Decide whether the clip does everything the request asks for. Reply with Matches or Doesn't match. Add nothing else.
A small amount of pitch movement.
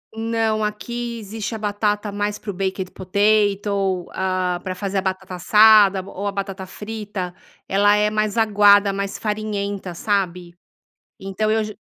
Matches